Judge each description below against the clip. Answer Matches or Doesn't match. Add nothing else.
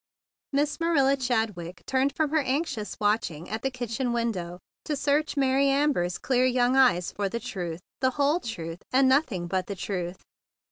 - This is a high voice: Matches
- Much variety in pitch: Matches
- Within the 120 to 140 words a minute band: Doesn't match